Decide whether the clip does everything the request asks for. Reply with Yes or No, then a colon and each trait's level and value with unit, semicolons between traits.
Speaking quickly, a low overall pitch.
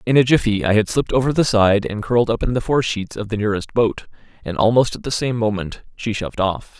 Yes: fast, 255 wpm; low, 110 Hz